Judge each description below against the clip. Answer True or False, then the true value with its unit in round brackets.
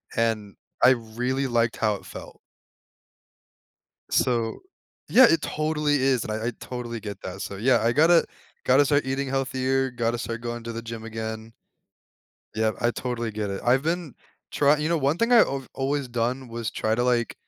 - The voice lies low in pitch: True (120 Hz)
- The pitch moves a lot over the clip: False (3.0 semitones)